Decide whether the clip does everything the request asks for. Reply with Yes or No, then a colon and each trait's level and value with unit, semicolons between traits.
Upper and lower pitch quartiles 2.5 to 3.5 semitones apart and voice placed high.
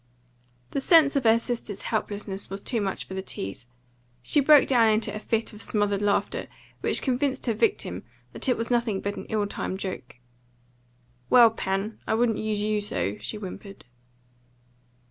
Yes: average, 3.1 semitones; high, 215 Hz